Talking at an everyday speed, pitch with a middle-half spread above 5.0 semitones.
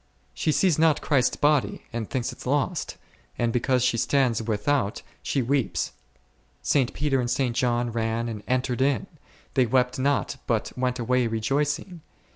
No: average, 155 wpm; average, 3.2 semitones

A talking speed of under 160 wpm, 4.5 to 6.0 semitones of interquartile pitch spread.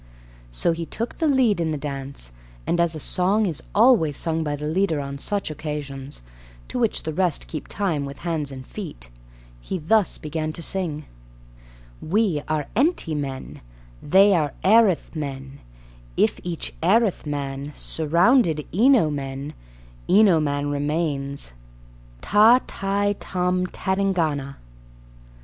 Yes: slow, 135 wpm; average, 5.2 semitones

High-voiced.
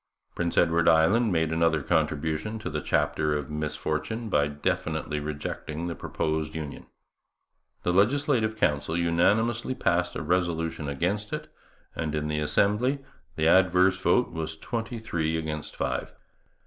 No: very low, 80 Hz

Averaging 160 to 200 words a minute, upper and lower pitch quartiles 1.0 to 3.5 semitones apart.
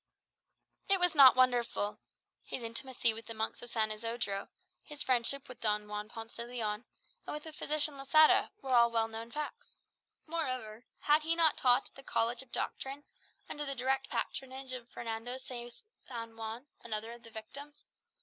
Yes: average, 175 wpm; average, 3.2 semitones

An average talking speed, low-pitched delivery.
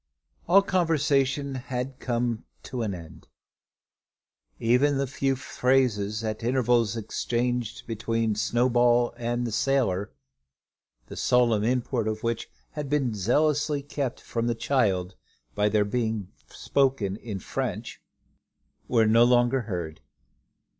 No: slow, 120 wpm; low, 120 Hz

